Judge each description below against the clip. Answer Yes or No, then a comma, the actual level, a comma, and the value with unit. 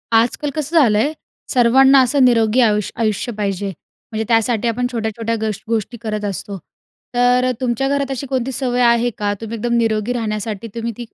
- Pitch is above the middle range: Yes, high, 235 Hz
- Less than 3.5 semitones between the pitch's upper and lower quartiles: Yes, narrow, 2.5 semitones